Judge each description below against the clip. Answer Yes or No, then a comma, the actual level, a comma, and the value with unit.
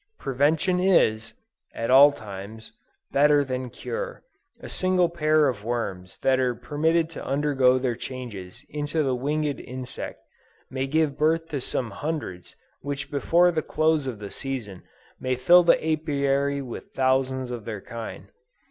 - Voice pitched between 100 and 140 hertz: Yes, low, 135 Hz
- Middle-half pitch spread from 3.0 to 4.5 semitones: Yes, average, 3.8 semitones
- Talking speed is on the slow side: No, average, 150 wpm